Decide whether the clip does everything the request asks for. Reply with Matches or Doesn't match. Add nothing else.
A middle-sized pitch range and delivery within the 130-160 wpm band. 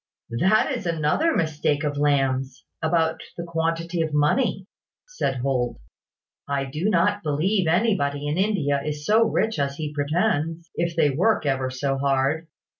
Matches